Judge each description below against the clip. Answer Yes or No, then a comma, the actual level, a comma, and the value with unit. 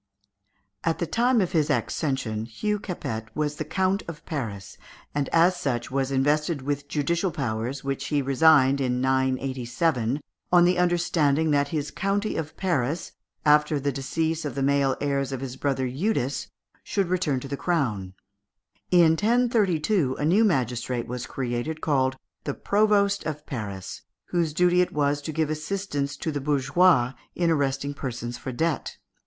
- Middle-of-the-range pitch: Yes, medium, 145 Hz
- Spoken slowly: No, average, 155 wpm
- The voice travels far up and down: No, average, 4.4 semitones